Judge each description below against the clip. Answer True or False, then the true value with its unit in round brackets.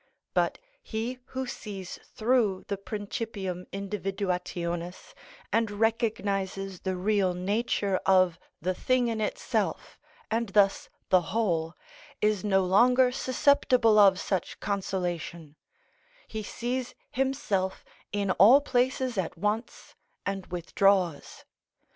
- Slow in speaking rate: True (105 wpm)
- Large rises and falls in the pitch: False (3.5 semitones)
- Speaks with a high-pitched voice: True (200 Hz)